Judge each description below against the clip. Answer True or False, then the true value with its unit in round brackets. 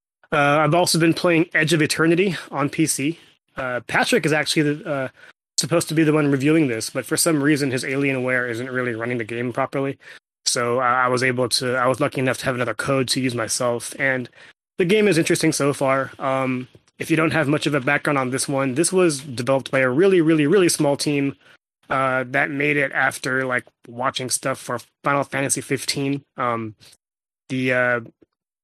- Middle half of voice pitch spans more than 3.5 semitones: False (3.1 semitones)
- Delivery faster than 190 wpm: True (200 wpm)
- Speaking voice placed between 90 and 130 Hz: False (140 Hz)